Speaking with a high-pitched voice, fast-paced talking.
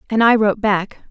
Yes: high, 210 Hz; fast, 215 wpm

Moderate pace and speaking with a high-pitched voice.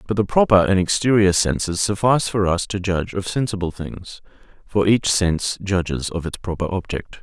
No: average, 185 wpm; very low, 95 Hz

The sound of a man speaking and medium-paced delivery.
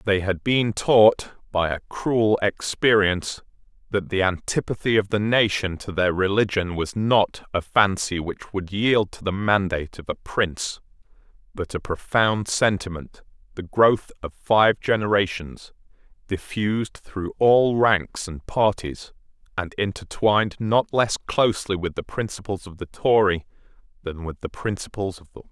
Yes: male; average, 150 wpm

